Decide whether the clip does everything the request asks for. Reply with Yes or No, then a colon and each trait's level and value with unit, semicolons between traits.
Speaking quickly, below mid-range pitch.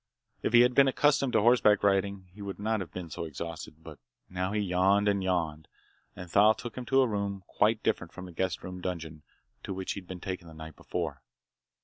Yes: fast, 215 wpm; very low, 95 Hz